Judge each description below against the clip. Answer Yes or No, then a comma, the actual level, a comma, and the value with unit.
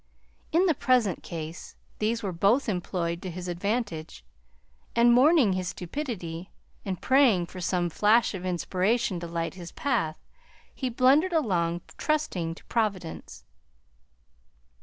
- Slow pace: Yes, slow, 130 wpm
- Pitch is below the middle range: No, high, 190 Hz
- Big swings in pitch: Yes, wide, 5.9 semitones